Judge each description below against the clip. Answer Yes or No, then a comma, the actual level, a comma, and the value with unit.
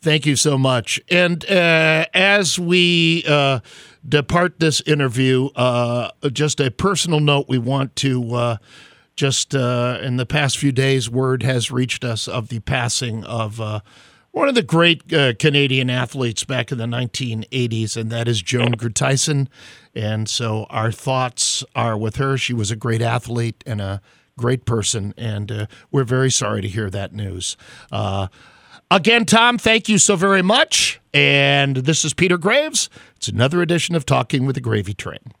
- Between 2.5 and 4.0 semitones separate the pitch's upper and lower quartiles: No, average, 4.6 semitones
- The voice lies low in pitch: Yes, low, 130 Hz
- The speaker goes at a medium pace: Yes, average, 170 wpm